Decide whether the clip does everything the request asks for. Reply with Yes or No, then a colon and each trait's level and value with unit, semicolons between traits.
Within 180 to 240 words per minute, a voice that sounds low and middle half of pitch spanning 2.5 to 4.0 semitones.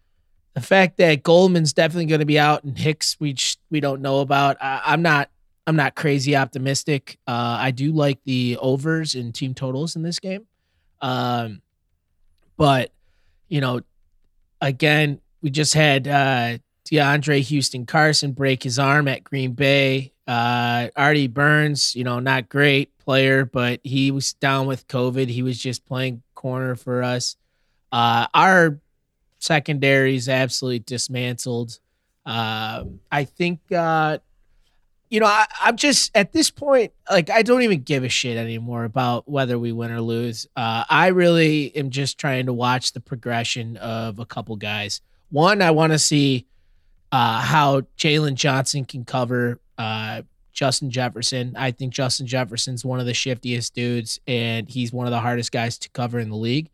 No: average, 165 wpm; low, 130 Hz; average, 3.5 semitones